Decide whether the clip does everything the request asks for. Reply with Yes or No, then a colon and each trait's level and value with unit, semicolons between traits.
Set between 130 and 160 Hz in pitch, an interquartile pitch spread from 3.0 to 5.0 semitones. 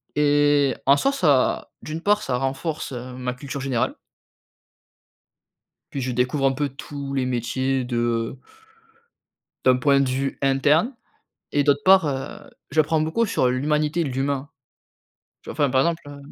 No: medium, 140 Hz; narrow, 2.4 semitones